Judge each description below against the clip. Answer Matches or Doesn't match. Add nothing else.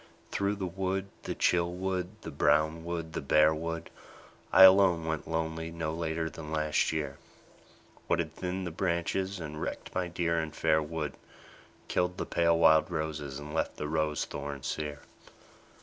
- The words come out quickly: Doesn't match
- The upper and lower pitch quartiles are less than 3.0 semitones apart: Matches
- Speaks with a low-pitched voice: Matches